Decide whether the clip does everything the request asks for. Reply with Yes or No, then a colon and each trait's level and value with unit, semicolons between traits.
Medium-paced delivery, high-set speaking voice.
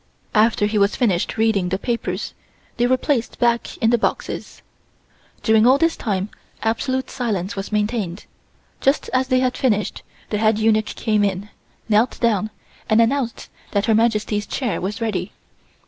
Yes: average, 160 wpm; high, 220 Hz